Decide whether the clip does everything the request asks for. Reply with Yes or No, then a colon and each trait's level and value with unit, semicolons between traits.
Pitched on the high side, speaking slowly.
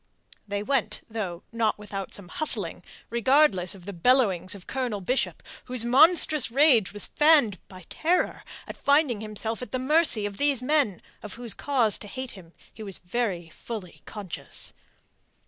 No: high, 225 Hz; average, 160 wpm